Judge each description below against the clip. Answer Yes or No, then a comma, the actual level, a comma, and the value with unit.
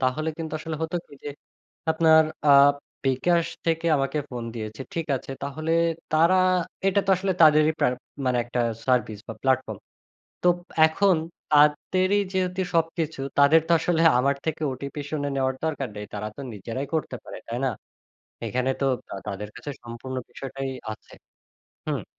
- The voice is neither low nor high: Yes, medium, 145 Hz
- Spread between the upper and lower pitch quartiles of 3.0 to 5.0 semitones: Yes, average, 4.1 semitones